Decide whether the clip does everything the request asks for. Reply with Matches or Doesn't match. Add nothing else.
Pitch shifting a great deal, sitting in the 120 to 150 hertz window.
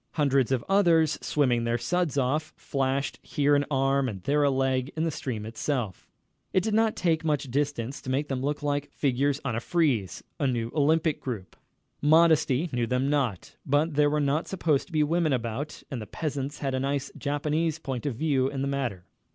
Doesn't match